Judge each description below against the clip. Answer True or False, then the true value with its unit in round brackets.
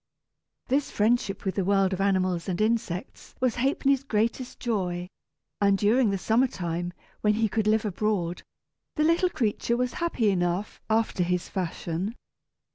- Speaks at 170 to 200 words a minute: False (150 wpm)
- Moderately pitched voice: False (210 Hz)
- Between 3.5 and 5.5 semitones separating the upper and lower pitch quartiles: True (4.2 semitones)